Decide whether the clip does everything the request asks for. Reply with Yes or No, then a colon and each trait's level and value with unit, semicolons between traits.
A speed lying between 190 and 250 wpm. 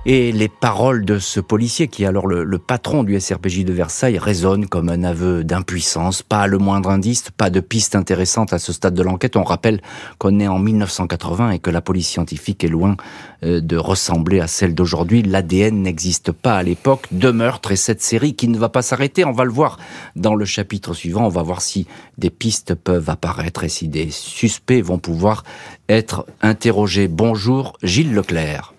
Yes: average, 195 wpm